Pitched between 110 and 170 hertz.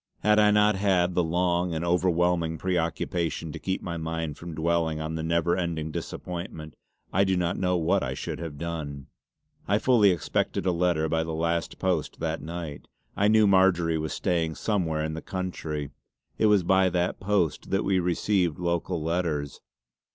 No: very low, 85 Hz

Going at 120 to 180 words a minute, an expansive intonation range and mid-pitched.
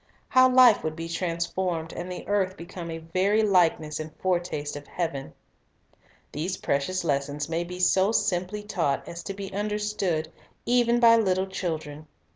No: average, 155 wpm; average, 3.7 semitones; medium, 180 Hz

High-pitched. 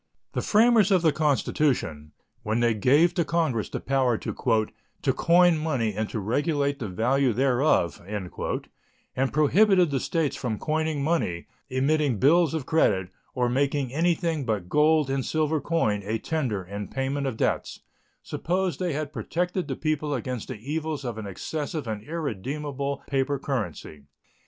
No: medium, 140 Hz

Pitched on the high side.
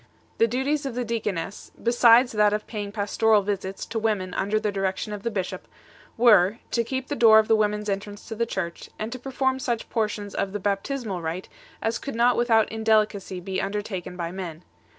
Yes: high, 215 Hz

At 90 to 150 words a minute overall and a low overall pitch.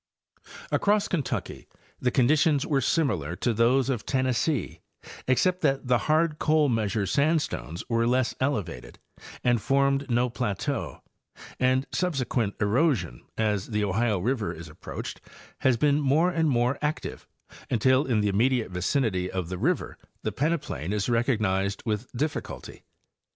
Yes: average, 140 wpm; low, 125 Hz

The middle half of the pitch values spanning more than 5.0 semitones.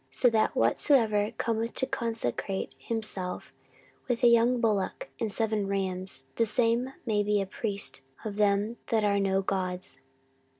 No: average, 2.8 semitones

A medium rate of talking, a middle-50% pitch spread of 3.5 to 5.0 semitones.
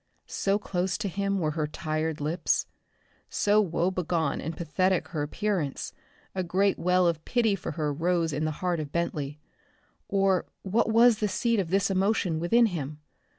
Yes: average, 170 wpm; average, 3.8 semitones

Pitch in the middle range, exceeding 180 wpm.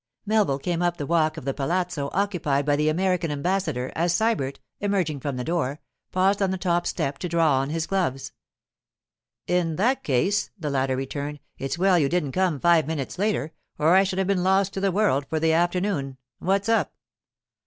Yes: medium, 170 Hz; average, 195 wpm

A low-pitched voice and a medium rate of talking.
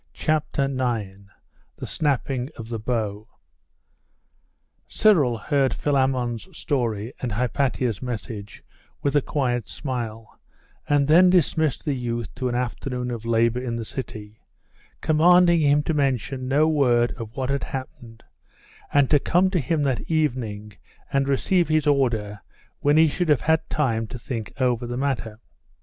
Yes: low, 130 Hz; average, 145 wpm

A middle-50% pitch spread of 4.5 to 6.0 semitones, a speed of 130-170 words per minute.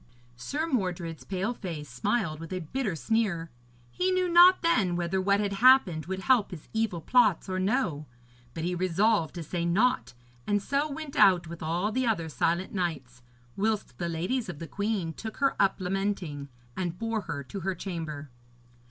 No: average, 5.1 semitones; average, 180 wpm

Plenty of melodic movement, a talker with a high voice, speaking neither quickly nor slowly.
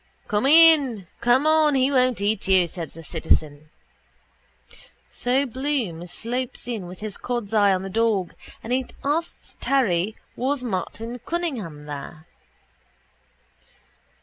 No: wide, 6.2 semitones; high, 230 Hz; slow, 125 wpm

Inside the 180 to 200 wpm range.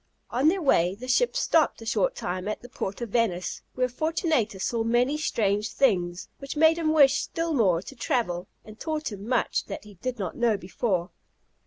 Yes: average, 195 wpm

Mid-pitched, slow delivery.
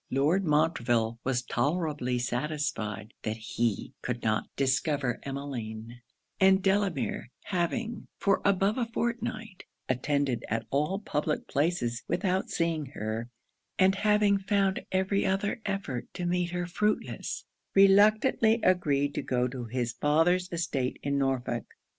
Yes: medium, 150 Hz; slow, 125 wpm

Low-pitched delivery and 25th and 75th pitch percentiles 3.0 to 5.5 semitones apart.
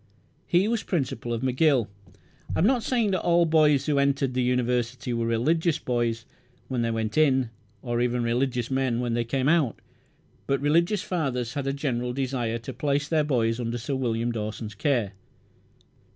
Yes: low, 130 Hz; average, 4.0 semitones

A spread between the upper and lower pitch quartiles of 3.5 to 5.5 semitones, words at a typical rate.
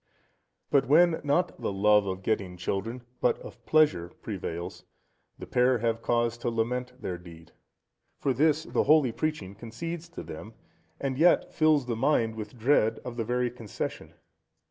Yes: average, 5.1 semitones; average, 160 wpm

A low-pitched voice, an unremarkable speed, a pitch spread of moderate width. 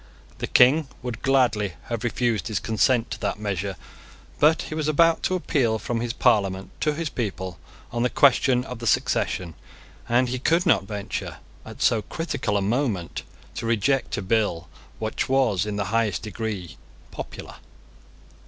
Yes: low, 115 Hz; average, 160 wpm; average, 4.3 semitones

